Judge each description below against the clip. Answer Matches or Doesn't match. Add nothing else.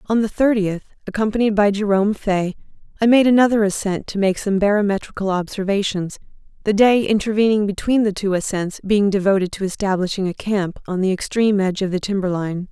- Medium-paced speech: Matches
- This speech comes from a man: Doesn't match